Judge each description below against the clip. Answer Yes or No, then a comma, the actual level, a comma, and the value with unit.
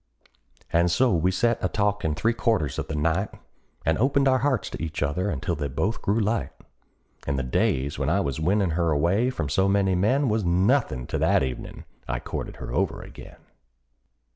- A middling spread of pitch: No, wide, 6.2 semitones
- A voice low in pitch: Yes, very low, 90 Hz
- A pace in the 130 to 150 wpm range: No, average, 190 wpm